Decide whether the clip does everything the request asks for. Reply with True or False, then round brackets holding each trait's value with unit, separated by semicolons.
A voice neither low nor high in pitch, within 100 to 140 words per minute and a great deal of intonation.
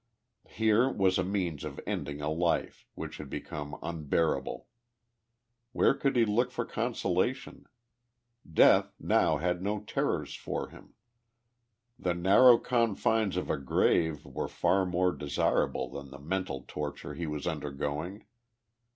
False (90 Hz; 135 wpm; 5.9 semitones)